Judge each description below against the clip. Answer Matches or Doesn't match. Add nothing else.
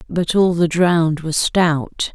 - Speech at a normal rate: Matches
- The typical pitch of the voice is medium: Matches